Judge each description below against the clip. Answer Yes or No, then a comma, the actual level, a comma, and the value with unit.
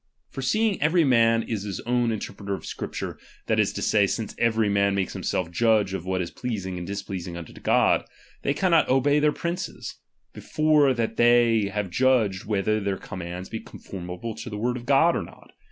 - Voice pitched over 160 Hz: No, low, 110 Hz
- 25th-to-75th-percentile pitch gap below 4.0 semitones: No, average, 4.8 semitones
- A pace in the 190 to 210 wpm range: Yes, average, 200 wpm